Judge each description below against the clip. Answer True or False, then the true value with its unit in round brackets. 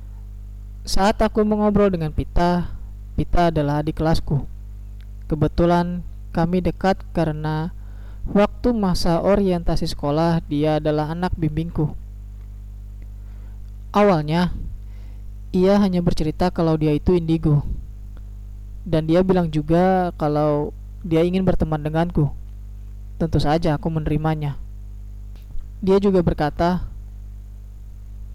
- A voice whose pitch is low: False (155 Hz)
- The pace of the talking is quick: False (95 wpm)